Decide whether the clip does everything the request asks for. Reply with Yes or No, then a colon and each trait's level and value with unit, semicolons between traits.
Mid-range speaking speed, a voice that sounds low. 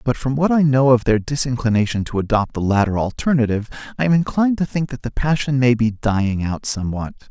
No: fast, 215 wpm; low, 125 Hz